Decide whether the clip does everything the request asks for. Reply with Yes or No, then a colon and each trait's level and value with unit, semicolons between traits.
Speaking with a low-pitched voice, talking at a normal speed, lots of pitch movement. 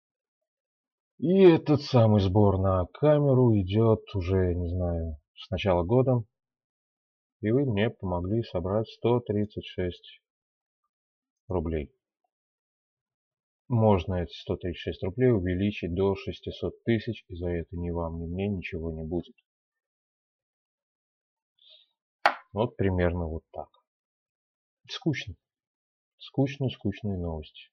No: low, 105 Hz; slow, 105 wpm; wide, 6.2 semitones